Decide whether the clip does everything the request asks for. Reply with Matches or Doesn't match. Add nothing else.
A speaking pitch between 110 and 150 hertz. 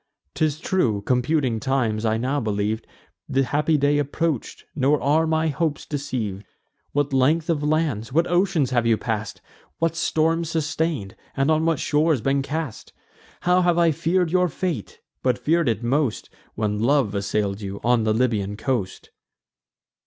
Matches